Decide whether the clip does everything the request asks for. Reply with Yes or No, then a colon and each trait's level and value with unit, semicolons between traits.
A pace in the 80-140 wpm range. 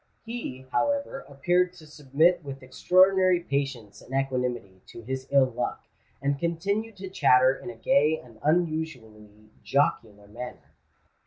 Yes: slow, 135 wpm